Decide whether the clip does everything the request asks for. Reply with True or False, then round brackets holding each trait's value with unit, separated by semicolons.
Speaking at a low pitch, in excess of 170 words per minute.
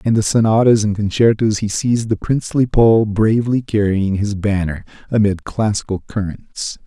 False (105 Hz; 150 wpm)